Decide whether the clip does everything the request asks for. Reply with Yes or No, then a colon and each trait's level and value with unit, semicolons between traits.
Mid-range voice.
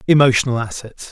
No: low, 125 Hz